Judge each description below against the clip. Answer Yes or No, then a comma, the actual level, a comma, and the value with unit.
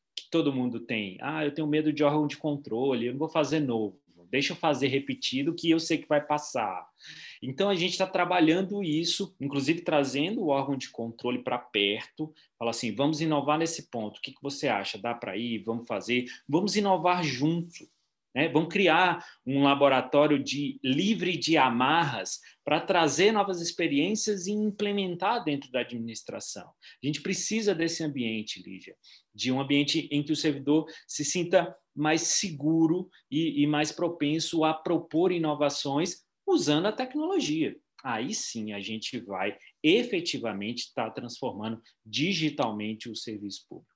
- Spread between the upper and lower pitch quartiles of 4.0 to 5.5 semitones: Yes, average, 4.8 semitones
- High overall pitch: No, medium, 150 Hz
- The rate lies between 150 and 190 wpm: Yes, average, 160 wpm